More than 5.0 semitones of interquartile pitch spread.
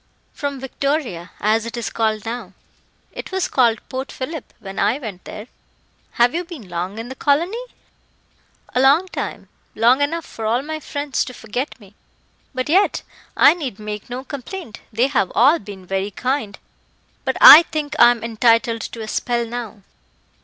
No: average, 4.7 semitones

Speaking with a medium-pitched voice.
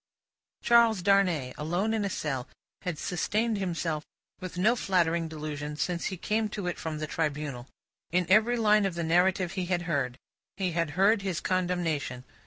Yes: medium, 180 Hz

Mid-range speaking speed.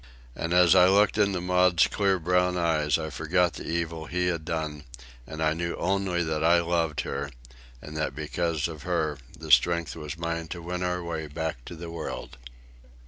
Yes: average, 190 wpm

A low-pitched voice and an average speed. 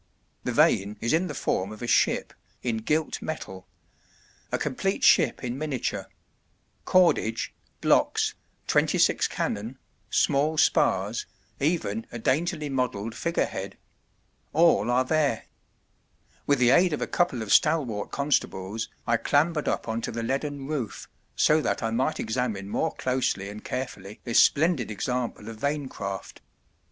Yes: low, 125 Hz; average, 145 wpm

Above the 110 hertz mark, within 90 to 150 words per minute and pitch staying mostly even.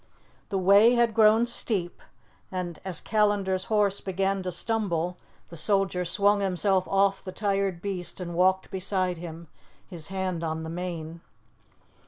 Yes: high, 190 Hz; average, 145 wpm; narrow, 2.3 semitones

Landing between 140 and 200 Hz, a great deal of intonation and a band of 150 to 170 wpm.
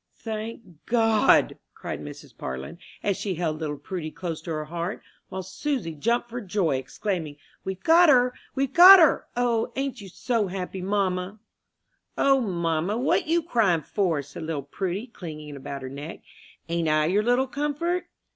Yes: high, 190 Hz; wide, 6.9 semitones; average, 165 wpm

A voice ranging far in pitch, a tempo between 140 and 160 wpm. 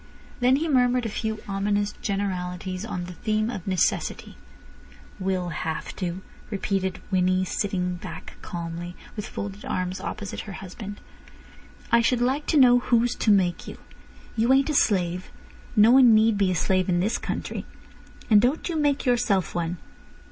No: average, 4.4 semitones; average, 155 wpm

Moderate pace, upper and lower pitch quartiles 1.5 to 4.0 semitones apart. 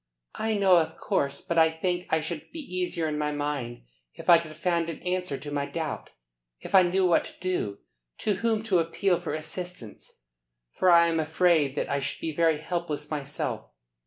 Yes: average, 195 wpm; average, 3.2 semitones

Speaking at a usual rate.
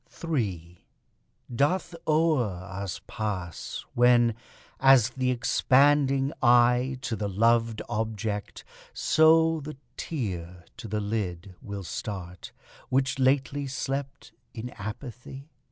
No: slow, 105 wpm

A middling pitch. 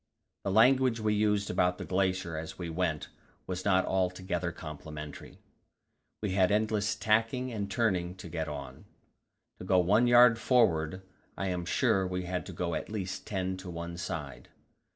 No: very low, 95 Hz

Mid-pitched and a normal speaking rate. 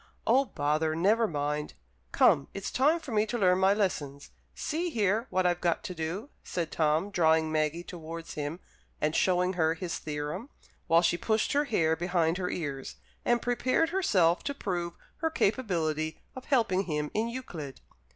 Yes: medium, 180 Hz; average, 170 wpm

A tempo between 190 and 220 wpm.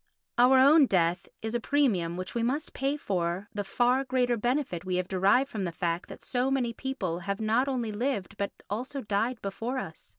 Yes: average, 200 wpm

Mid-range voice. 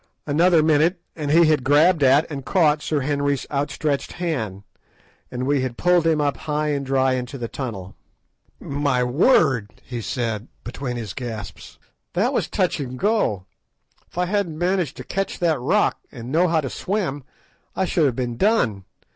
Yes: medium, 145 Hz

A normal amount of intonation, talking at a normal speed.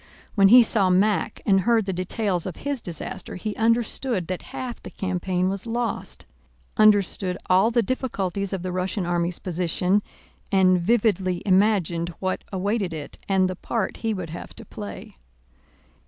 Yes: average, 3.1 semitones; average, 155 wpm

